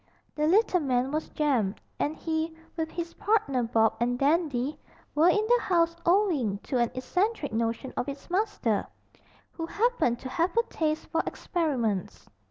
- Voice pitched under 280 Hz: No, very high, 310 Hz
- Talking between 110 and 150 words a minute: No, average, 160 wpm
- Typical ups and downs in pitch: No, wide, 6.1 semitones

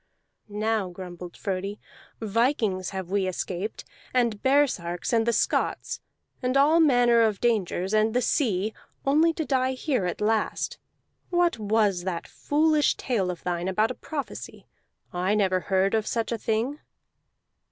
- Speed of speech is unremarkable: Yes, average, 145 wpm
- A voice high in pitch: Yes, high, 220 Hz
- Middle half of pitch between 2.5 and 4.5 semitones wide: No, average, 5.2 semitones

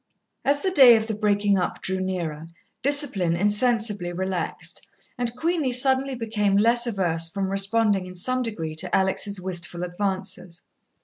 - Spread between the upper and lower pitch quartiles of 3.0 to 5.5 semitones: Yes, average, 4.5 semitones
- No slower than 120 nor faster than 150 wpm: Yes, average, 145 wpm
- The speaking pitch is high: Yes, high, 200 Hz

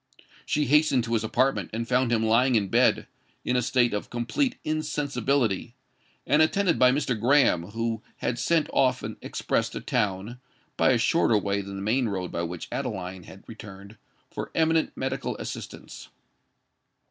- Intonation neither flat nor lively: Yes, average, 4.6 semitones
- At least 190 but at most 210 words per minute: No, average, 160 wpm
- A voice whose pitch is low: Yes, low, 120 Hz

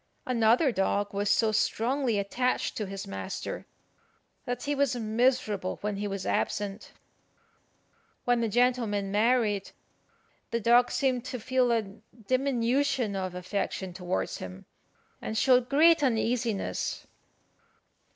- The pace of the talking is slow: Yes, slow, 120 wpm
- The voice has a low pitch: No, high, 230 Hz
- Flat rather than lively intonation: No, average, 3.9 semitones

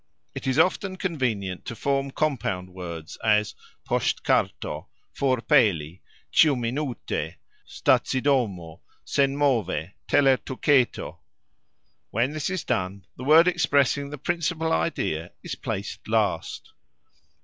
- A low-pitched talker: Yes, low, 130 Hz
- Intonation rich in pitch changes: Yes, wide, 7.0 semitones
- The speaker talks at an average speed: No, slow, 95 wpm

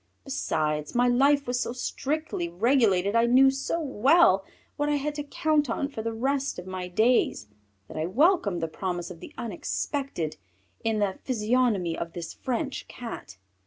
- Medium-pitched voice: No, high, 235 Hz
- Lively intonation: Yes, wide, 7.1 semitones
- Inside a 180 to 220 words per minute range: No, average, 165 wpm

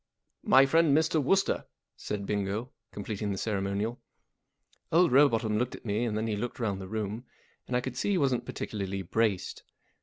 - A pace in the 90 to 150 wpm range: No, average, 180 wpm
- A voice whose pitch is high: No, low, 110 Hz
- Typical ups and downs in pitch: Yes, average, 4.3 semitones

